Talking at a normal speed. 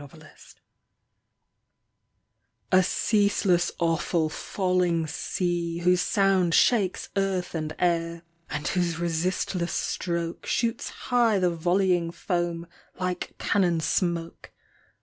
No: slow, 95 wpm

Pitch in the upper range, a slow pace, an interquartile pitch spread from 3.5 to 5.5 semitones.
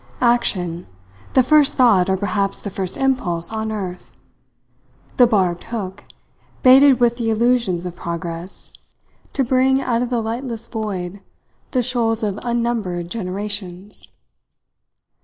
Yes: high, 220 Hz; slow, 125 wpm; average, 4.8 semitones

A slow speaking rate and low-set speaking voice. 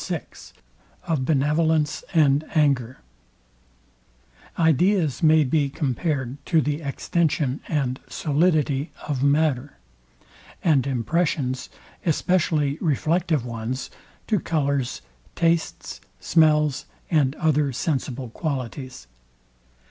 No: slow, 85 wpm; medium, 150 Hz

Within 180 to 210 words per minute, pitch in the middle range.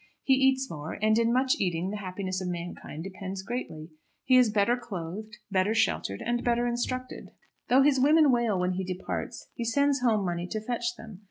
No: average, 190 wpm; high, 215 Hz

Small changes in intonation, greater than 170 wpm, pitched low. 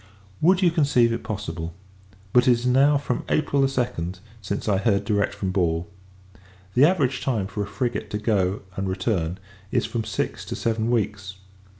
No: average, 4.5 semitones; average, 180 wpm; low, 110 Hz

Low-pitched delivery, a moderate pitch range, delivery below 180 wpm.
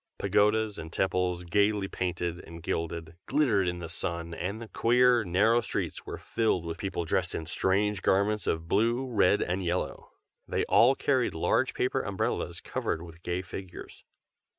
Yes: very low, 95 Hz; average, 3.9 semitones; average, 160 wpm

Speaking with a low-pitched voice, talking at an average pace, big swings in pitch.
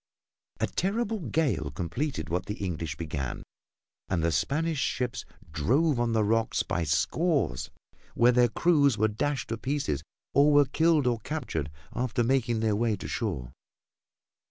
Yes: low, 115 Hz; average, 150 wpm; wide, 8.5 semitones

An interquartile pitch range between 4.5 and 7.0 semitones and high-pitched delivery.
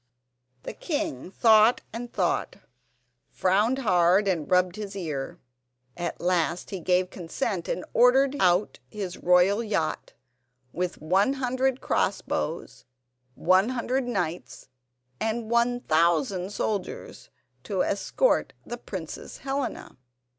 Yes: average, 5.1 semitones; high, 195 Hz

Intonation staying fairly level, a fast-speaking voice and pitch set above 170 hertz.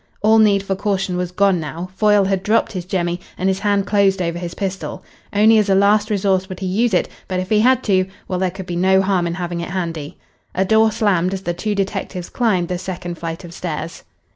Yes: narrow, 2.3 semitones; fast, 235 wpm; high, 190 Hz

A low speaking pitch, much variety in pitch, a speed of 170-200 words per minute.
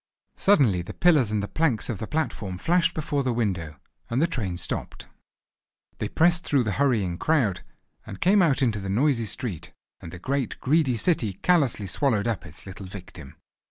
Yes: low, 115 Hz; wide, 7.4 semitones; average, 180 wpm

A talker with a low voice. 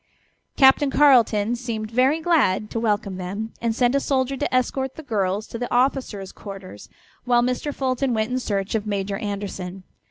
No: high, 230 Hz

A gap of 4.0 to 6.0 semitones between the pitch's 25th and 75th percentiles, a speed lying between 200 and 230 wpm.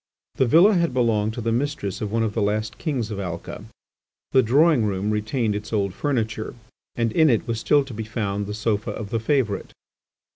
No: average, 3.5 semitones; fast, 205 wpm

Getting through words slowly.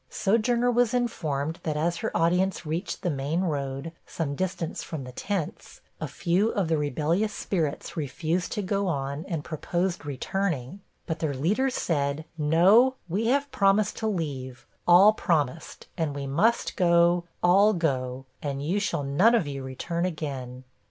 No: average, 160 wpm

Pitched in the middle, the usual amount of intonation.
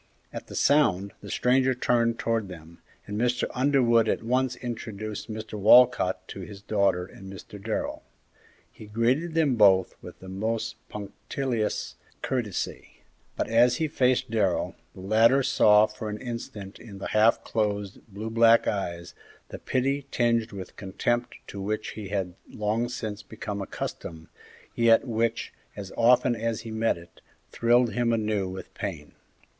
No: low, 110 Hz; average, 3.1 semitones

